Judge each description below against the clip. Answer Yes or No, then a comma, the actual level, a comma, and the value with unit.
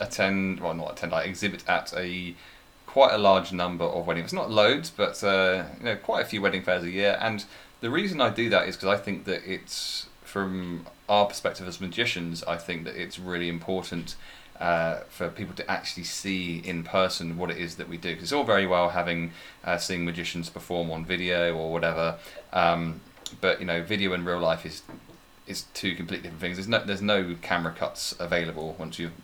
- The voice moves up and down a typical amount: No, narrow, 1.9 semitones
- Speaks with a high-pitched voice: No, very low, 90 Hz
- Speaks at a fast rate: Yes, fast, 210 wpm